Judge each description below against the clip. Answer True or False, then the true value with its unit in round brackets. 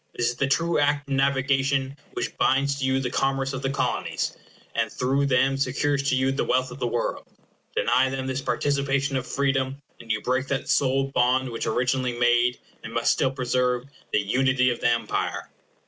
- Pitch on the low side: True (130 Hz)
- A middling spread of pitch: False (1.4 semitones)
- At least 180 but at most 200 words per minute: True (195 wpm)